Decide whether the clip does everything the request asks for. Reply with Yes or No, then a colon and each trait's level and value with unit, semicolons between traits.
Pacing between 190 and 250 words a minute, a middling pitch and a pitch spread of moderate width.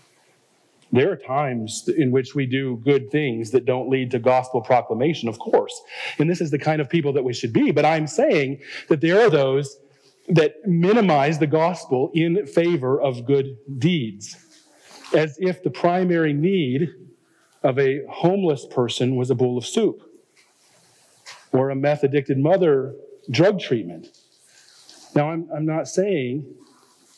No: average, 155 wpm; medium, 145 Hz; average, 4.1 semitones